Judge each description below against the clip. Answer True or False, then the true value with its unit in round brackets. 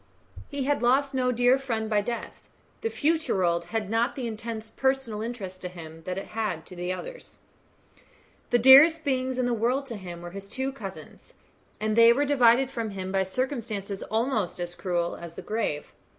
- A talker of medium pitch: False (225 Hz)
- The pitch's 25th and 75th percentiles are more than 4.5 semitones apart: True (5.5 semitones)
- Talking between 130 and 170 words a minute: False (185 wpm)